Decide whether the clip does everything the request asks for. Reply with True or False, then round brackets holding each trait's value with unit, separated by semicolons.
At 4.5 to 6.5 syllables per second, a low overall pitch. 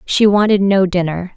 False (4.9 syllables/s; 190 Hz)